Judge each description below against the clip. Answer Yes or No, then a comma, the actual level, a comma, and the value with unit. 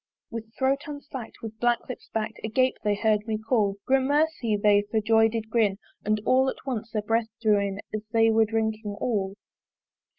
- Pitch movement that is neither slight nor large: No, narrow, 2.2 semitones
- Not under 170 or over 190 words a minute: Yes, average, 185 wpm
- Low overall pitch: No, high, 225 Hz